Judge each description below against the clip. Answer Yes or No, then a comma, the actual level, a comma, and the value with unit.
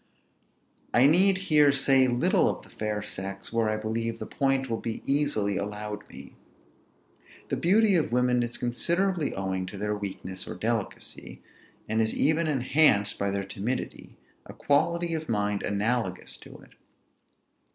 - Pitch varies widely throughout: Yes, wide, 5.8 semitones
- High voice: No, low, 115 Hz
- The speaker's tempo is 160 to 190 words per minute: No, average, 150 wpm